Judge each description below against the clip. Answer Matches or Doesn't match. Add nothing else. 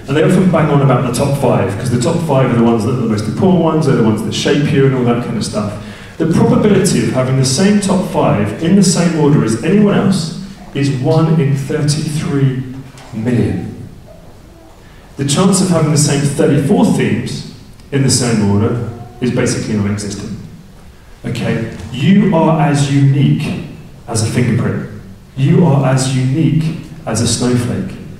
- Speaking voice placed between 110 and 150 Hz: Matches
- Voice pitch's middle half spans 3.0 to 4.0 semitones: Doesn't match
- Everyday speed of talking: Matches